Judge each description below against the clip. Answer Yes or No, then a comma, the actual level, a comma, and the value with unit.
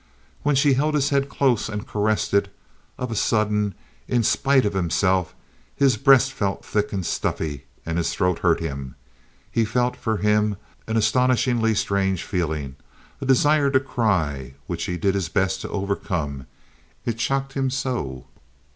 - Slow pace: No, average, 160 wpm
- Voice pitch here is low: Yes, low, 105 Hz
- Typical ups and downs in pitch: No, wide, 5.8 semitones